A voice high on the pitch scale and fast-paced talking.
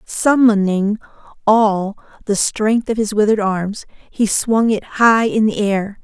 No: high, 210 Hz; average, 150 wpm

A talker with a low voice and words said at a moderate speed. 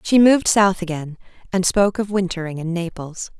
No: medium, 185 Hz; average, 175 wpm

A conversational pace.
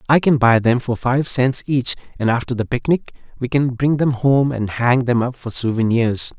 No: fast, 215 wpm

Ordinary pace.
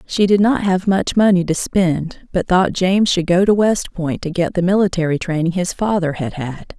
No: fast, 220 wpm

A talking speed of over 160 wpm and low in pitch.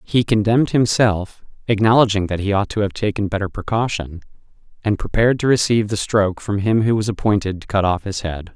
Yes: average, 195 wpm; low, 105 Hz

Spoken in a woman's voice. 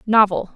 Yes: female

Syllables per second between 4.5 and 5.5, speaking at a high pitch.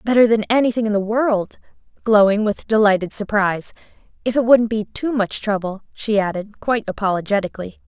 No: 5.8 syllables/s; high, 215 Hz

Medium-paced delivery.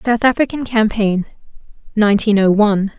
No: slow, 120 wpm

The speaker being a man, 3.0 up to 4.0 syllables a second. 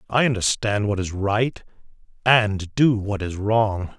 Yes: male; 3.8 syllables/s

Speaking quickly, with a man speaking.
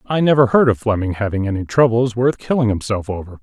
Yes: fast, 210 wpm; male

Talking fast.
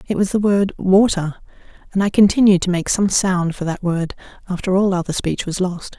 Yes: fast, 210 wpm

